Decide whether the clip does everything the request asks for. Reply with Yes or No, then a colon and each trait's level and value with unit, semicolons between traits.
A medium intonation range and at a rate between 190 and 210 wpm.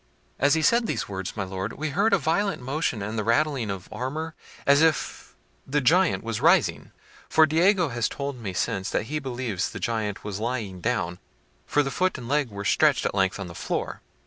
No: wide, 7.0 semitones; fast, 205 wpm